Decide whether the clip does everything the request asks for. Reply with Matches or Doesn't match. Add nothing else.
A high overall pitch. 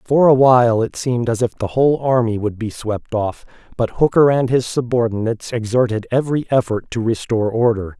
Doesn't match